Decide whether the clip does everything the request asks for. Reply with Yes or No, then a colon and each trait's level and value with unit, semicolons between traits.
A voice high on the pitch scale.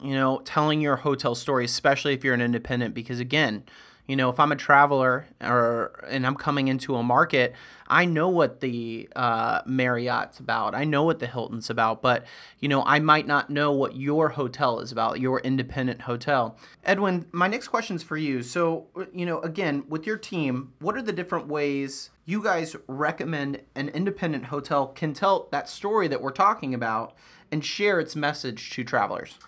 No: medium, 140 Hz